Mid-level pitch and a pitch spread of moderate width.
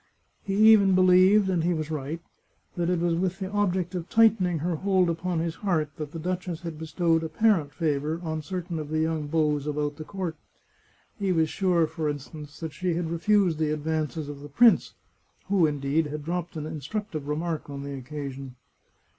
Yes: medium, 165 Hz; average, 3.2 semitones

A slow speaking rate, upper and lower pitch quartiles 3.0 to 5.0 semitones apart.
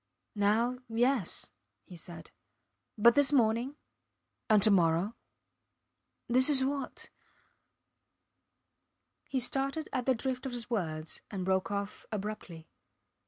Yes: slow, 115 wpm; average, 4.7 semitones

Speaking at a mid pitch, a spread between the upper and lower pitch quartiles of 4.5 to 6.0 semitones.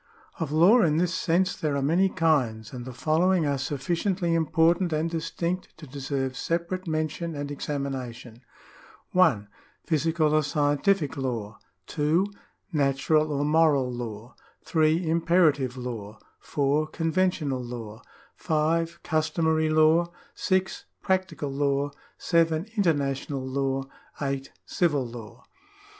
No: medium, 155 Hz; average, 3.6 semitones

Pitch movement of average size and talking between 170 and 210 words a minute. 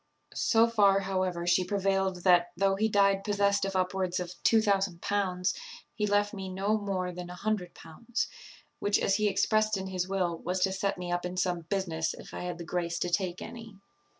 No: narrow, 2.1 semitones; average, 190 wpm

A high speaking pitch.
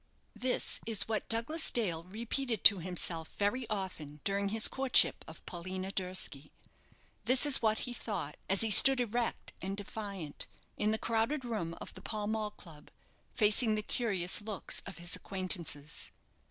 Yes: high, 205 Hz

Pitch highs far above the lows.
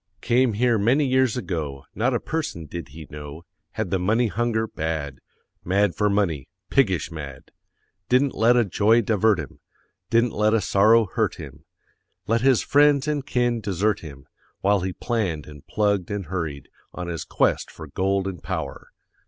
Yes: wide, 6.0 semitones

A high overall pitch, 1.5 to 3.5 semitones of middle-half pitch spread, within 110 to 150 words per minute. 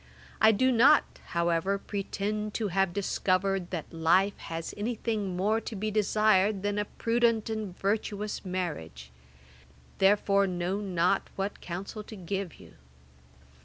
Yes: high, 200 Hz; narrow, 2.6 semitones; slow, 135 wpm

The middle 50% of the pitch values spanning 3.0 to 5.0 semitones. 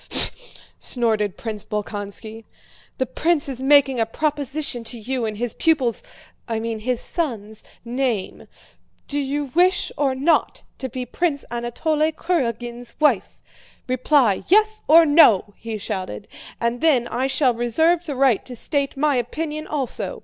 Yes: average, 4.6 semitones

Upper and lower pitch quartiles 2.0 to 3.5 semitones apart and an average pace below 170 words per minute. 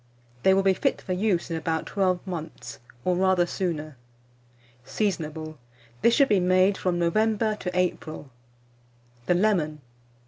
Yes: average, 3.1 semitones; average, 140 wpm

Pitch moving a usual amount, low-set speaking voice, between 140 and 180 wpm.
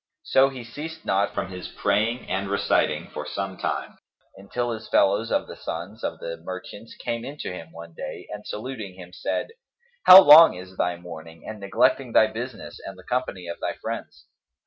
No: average, 4.9 semitones; low, 100 Hz; average, 190 wpm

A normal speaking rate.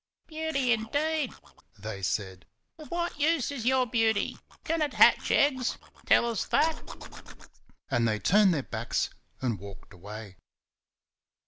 No: slow, 130 wpm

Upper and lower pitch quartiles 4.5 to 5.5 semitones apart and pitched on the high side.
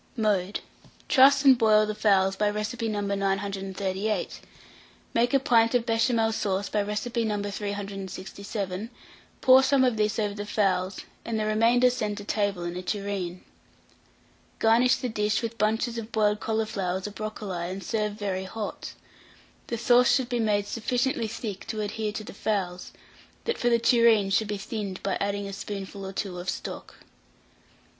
No: narrow, 2.5 semitones; high, 210 Hz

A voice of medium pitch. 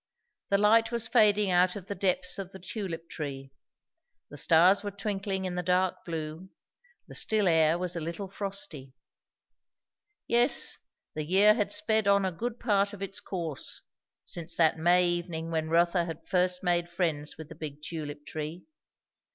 Yes: medium, 180 Hz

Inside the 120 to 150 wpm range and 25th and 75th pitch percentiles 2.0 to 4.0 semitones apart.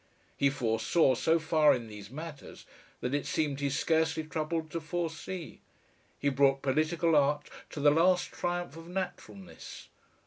Yes: average, 145 wpm; average, 3.1 semitones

